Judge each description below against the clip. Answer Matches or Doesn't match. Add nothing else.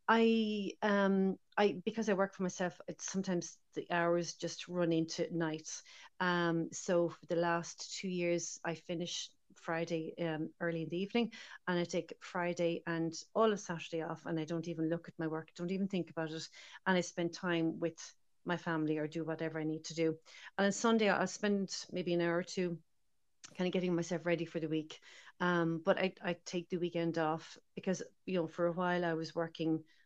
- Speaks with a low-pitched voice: Doesn't match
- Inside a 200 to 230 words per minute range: Matches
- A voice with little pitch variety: Matches